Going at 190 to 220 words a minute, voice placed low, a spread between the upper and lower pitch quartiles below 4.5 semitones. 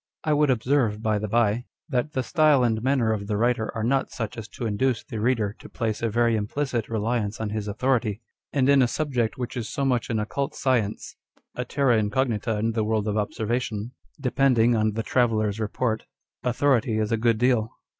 Yes: average, 200 wpm; low, 115 Hz; average, 2.8 semitones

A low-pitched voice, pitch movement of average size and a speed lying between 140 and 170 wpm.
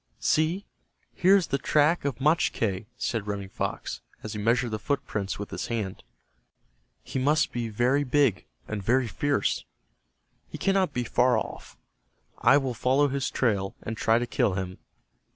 Yes: low, 125 Hz; average, 5.0 semitones; average, 160 wpm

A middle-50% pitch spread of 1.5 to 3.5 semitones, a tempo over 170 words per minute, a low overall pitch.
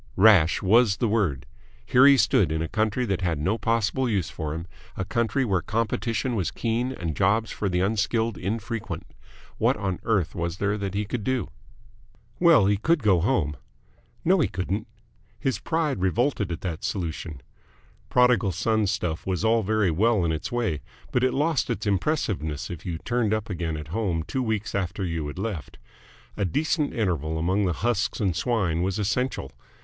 No: average, 4.7 semitones; average, 180 wpm; low, 100 Hz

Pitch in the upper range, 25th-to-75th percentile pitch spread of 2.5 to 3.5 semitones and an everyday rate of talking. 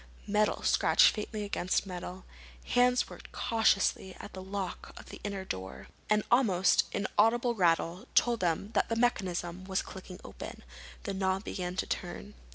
Yes: high, 195 Hz; average, 2.9 semitones; average, 155 wpm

